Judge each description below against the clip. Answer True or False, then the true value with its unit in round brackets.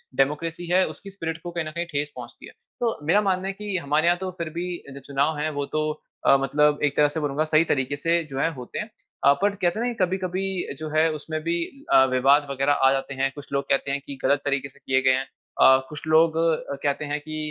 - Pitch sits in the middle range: True (150 Hz)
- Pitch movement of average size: True (3.4 semitones)